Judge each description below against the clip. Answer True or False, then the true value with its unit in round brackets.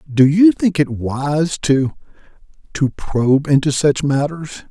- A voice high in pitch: False (145 Hz)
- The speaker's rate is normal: False (125 wpm)